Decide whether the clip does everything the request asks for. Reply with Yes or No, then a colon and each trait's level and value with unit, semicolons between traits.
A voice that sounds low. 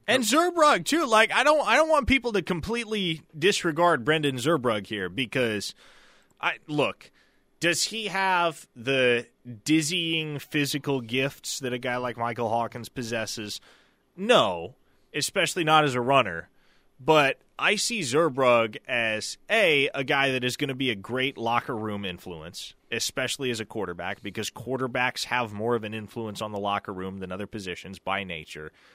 Yes: low, 130 Hz